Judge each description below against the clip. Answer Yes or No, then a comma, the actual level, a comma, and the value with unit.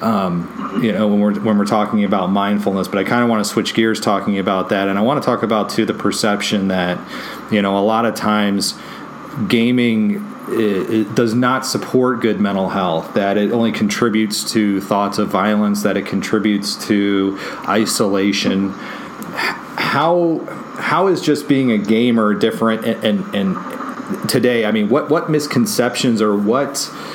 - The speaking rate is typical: Yes, average, 170 wpm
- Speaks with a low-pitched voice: Yes, low, 105 Hz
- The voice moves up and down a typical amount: Yes, average, 3.0 semitones